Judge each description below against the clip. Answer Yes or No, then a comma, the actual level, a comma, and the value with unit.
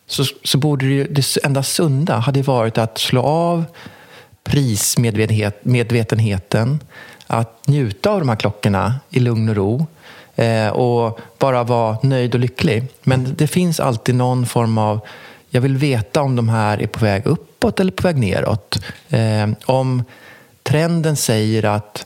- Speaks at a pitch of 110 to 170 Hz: Yes, low, 125 Hz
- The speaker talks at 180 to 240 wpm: No, average, 155 wpm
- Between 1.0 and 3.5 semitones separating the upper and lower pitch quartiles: No, average, 4.1 semitones